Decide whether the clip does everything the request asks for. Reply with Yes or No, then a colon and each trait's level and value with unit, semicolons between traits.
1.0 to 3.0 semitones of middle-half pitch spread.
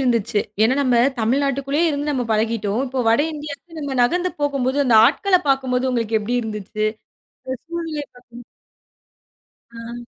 No: average, 3.7 semitones